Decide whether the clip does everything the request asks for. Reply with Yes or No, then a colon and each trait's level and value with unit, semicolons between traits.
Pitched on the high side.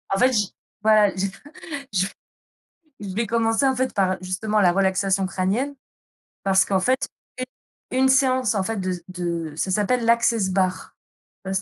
Yes: high, 200 Hz